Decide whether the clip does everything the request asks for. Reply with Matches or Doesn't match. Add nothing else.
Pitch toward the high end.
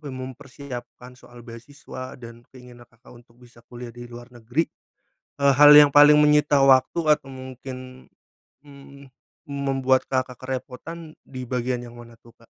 Doesn't match